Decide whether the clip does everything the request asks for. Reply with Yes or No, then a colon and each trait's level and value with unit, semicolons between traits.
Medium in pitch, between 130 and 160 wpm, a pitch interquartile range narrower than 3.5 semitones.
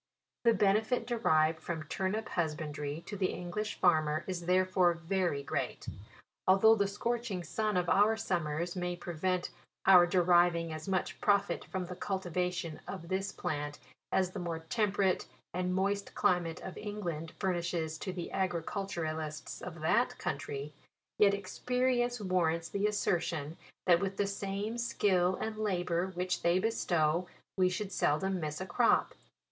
Yes: medium, 180 Hz; average, 150 wpm; average, 2.9 semitones